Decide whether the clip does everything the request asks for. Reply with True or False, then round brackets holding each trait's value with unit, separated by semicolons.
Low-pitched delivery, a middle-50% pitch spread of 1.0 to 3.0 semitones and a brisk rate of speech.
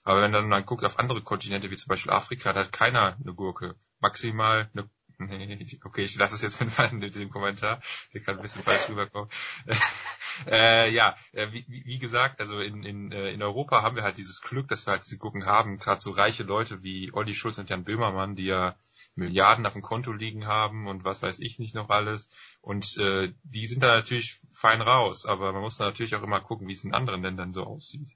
True (105 Hz; 2.5 semitones; 220 wpm)